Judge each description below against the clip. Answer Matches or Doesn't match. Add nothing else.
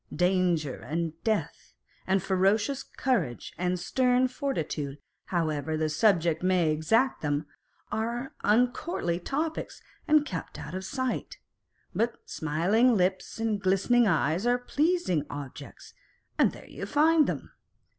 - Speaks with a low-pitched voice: Doesn't match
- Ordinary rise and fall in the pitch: Doesn't match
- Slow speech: Matches